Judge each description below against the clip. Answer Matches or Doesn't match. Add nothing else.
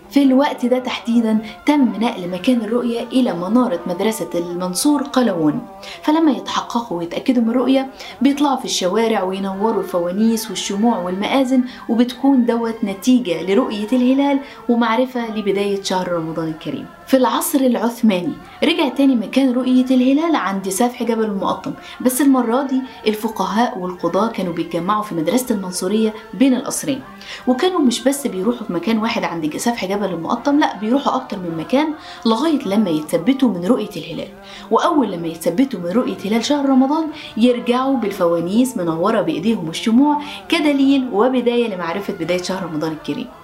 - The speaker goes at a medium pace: Doesn't match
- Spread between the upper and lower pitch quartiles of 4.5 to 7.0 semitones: Matches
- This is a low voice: Doesn't match